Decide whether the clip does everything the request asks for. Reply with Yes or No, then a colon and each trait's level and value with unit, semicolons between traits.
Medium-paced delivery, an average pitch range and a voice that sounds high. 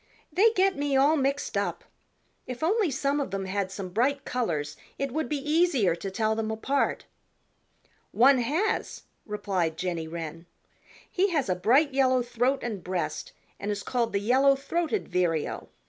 No: average, 160 wpm; wide, 6.7 semitones; very high, 250 Hz